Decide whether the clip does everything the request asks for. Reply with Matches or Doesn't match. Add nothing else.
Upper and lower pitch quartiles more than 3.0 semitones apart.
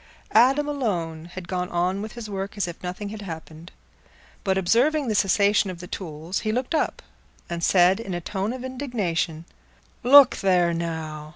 Matches